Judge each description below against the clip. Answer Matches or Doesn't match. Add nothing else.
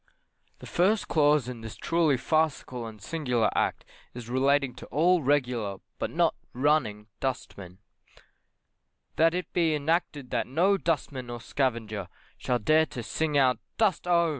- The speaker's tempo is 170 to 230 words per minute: Doesn't match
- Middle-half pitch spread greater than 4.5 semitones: Matches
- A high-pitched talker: Doesn't match